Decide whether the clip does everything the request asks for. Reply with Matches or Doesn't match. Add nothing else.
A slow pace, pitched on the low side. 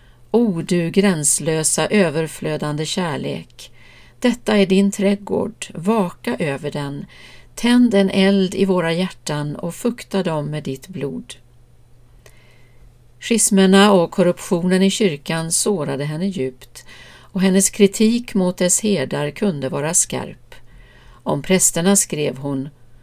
Doesn't match